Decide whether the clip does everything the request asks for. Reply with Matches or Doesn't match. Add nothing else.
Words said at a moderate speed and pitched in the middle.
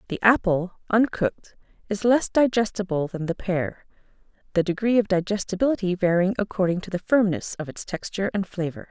Doesn't match